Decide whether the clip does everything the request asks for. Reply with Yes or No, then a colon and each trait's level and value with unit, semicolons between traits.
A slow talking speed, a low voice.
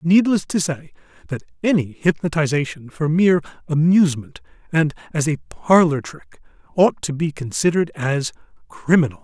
No: slow, 130 wpm; medium, 160 Hz